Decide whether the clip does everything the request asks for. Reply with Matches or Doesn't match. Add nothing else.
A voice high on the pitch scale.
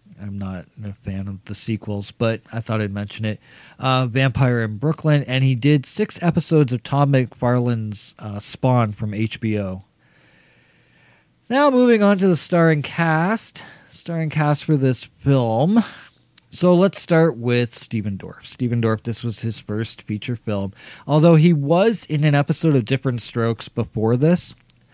Doesn't match